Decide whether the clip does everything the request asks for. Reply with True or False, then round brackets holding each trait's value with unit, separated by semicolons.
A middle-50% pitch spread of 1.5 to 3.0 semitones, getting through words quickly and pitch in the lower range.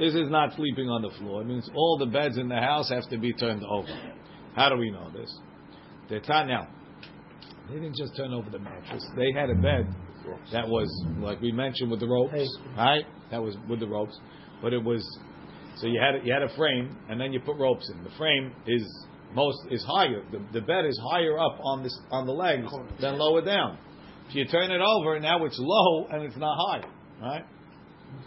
False (5.2 semitones; 215 wpm; 125 Hz)